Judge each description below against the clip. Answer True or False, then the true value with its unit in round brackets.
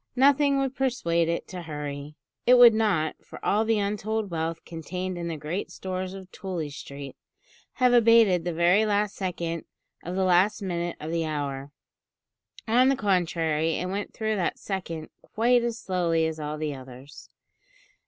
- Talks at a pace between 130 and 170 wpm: True (165 wpm)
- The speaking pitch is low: False (180 Hz)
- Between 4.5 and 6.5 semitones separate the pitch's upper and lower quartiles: True (4.9 semitones)